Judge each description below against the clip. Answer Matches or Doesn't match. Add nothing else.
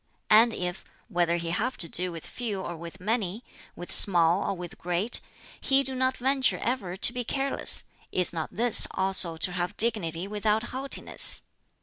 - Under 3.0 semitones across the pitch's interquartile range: Doesn't match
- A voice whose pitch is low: Doesn't match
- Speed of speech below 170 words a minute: Doesn't match